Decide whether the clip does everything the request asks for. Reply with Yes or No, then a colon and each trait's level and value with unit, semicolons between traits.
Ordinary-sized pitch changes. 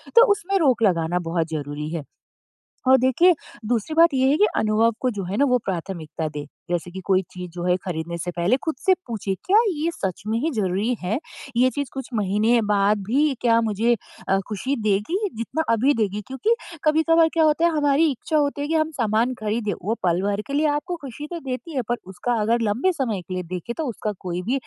No: wide, 7.0 semitones